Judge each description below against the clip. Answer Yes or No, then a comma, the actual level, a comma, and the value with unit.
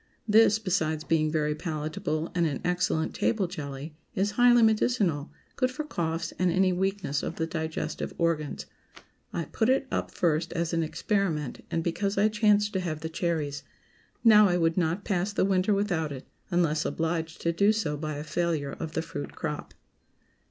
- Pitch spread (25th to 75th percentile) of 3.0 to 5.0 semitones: Yes, average, 4.1 semitones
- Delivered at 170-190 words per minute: Yes, average, 175 wpm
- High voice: No, medium, 170 Hz